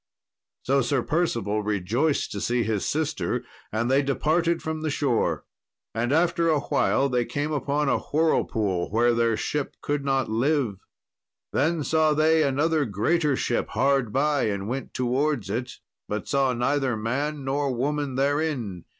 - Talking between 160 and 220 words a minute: No, average, 150 wpm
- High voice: No, low, 135 Hz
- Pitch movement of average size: Yes, average, 4.2 semitones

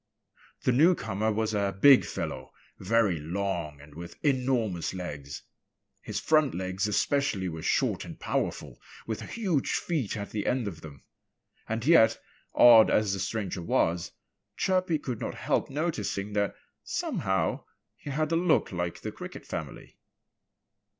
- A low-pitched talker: Yes, low, 105 Hz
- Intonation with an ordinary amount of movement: No, wide, 6.6 semitones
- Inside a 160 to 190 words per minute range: No, average, 145 wpm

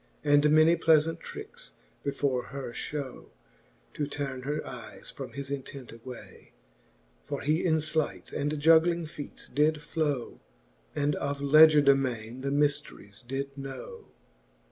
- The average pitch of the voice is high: No, medium, 145 Hz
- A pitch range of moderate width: No, narrow, 2.2 semitones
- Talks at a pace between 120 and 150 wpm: Yes, slow, 135 wpm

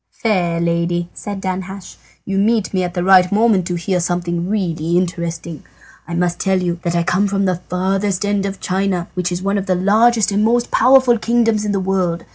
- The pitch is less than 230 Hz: Yes, medium, 185 Hz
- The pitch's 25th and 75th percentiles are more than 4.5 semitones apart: No, narrow, 2.6 semitones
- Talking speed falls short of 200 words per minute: No, fast, 205 wpm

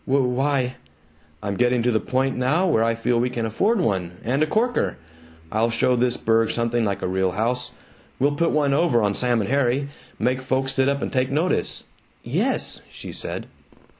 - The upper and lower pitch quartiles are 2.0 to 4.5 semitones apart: Yes, average, 3.4 semitones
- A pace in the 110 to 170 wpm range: No, average, 195 wpm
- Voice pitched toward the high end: No, low, 125 Hz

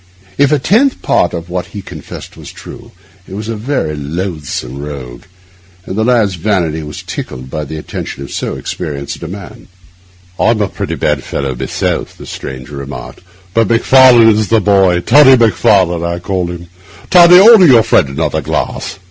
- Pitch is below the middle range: Yes, very low, 90 Hz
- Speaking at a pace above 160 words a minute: Yes, average, 170 wpm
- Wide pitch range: Yes, wide, 7.2 semitones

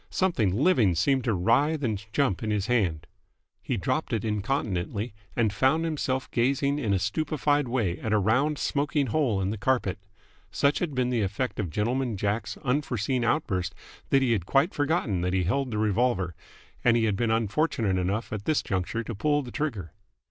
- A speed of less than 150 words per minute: No, average, 185 wpm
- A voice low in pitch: Yes, low, 115 Hz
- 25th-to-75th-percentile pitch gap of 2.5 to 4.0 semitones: No, wide, 5.4 semitones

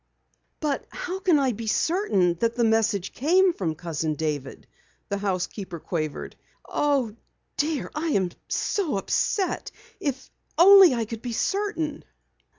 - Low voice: No, high, 235 Hz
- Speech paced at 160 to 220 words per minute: No, slow, 135 wpm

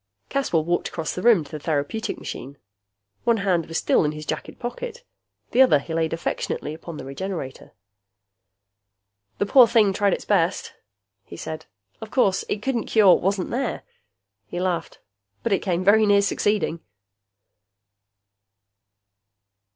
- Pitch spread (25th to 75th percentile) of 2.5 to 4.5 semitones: No, average, 5.2 semitones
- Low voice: No, high, 190 Hz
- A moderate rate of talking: Yes, average, 150 wpm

